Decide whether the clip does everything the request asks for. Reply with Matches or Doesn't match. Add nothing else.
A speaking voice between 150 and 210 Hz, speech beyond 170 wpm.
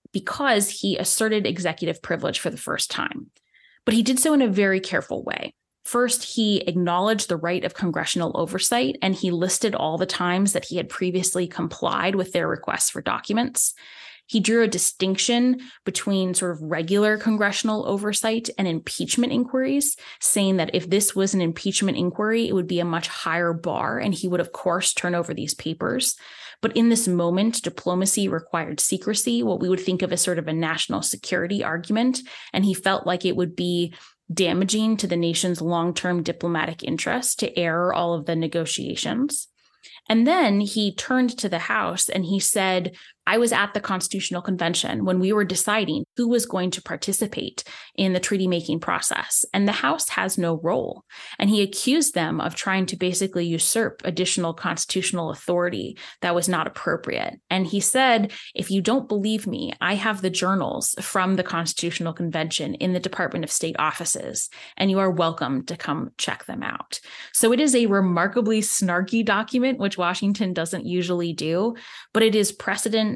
Matches